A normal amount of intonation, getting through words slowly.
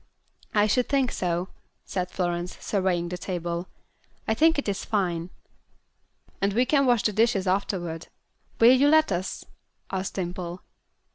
No: average, 4.6 semitones; average, 145 wpm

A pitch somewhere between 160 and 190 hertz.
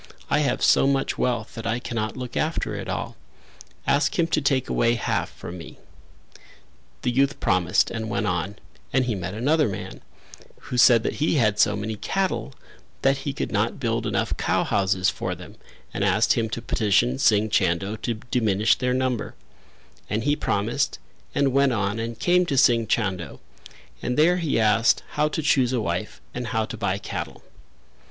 No: low, 115 Hz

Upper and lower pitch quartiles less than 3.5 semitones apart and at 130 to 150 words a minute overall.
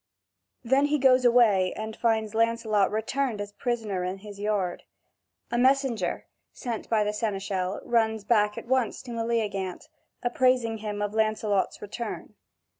Yes: narrow, 2.6 semitones; average, 140 wpm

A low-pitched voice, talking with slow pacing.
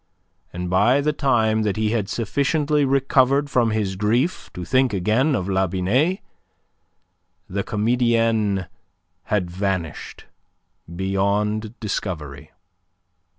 Yes: low, 110 Hz; slow, 110 wpm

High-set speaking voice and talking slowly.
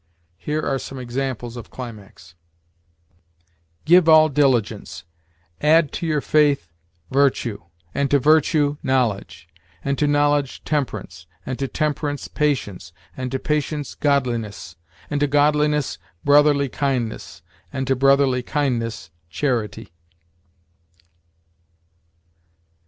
No: medium, 140 Hz; slow, 105 wpm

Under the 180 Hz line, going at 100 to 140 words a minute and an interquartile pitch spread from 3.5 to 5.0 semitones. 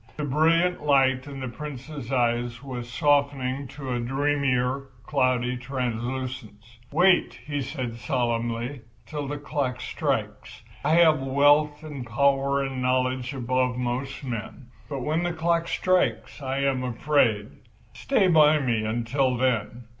No: low, 135 Hz; slow, 135 wpm; average, 2.8 semitones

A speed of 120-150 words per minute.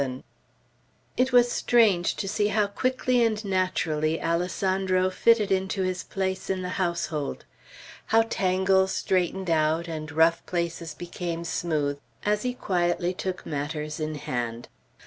Yes: slow, 135 wpm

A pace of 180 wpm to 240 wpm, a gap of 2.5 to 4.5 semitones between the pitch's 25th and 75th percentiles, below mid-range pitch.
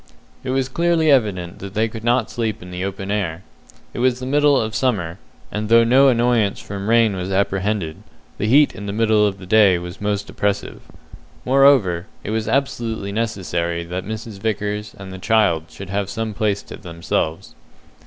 Yes: average, 185 wpm; average, 3.3 semitones; low, 105 Hz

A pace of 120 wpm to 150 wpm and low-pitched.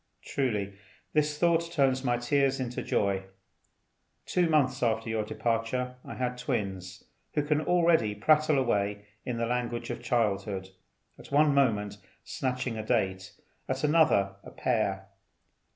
Yes: slow, 135 wpm; low, 120 Hz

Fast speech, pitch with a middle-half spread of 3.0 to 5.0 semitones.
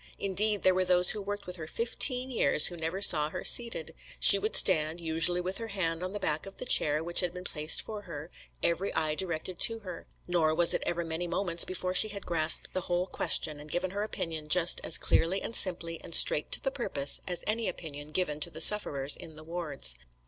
Yes: fast, 225 wpm; average, 3.4 semitones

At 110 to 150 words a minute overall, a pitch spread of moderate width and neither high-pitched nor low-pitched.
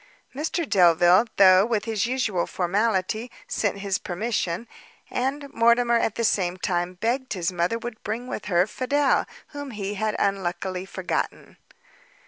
No: average, 140 wpm; average, 4.4 semitones; high, 210 Hz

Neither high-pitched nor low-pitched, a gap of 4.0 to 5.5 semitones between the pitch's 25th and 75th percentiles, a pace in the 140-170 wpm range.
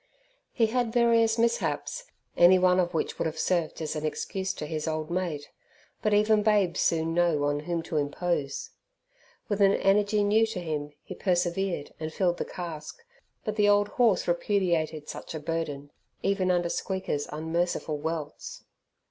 Yes: medium, 175 Hz; average, 4.4 semitones; average, 165 wpm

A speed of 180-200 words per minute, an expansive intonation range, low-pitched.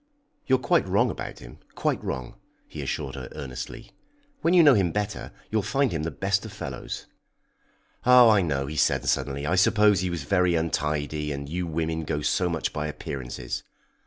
Yes: average, 190 wpm; wide, 5.8 semitones; very low, 80 Hz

